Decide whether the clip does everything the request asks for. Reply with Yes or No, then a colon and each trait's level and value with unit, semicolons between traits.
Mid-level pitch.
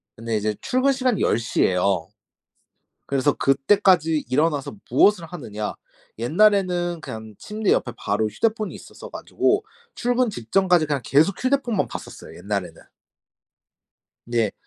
Yes: medium, 160 Hz